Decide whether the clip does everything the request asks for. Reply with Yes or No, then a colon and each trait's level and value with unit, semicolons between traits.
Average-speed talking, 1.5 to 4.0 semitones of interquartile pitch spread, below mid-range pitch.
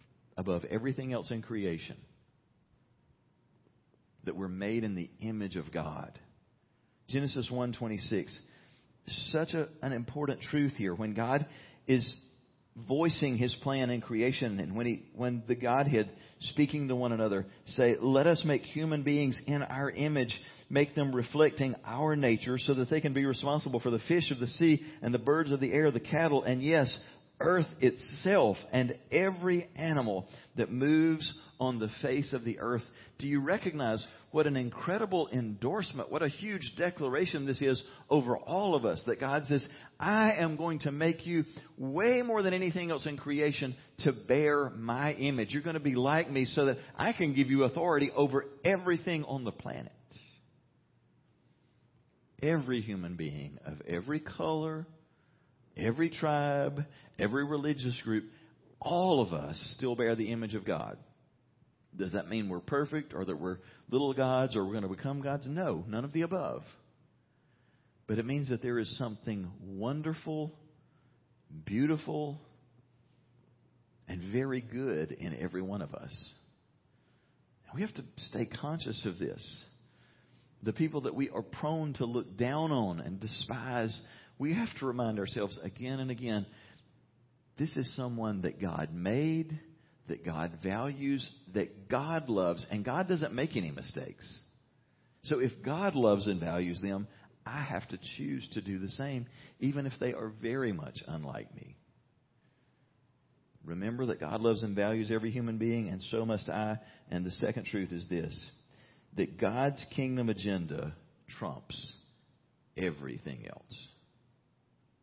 No: average, 155 wpm; average, 4.7 semitones; low, 130 Hz